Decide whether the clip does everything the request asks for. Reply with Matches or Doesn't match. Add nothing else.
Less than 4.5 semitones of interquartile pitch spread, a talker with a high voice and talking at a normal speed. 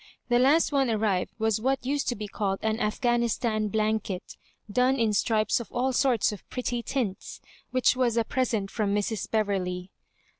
Matches